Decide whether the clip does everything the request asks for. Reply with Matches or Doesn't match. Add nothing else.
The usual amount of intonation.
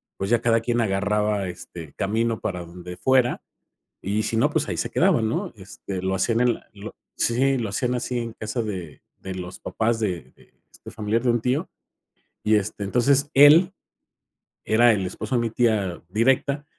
Matches